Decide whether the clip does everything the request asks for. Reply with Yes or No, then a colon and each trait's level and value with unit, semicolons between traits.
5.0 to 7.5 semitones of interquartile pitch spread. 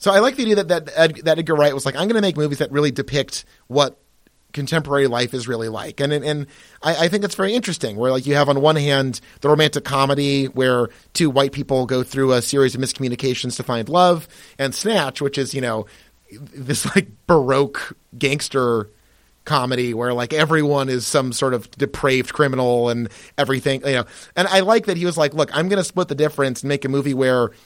No: average, 3.2 semitones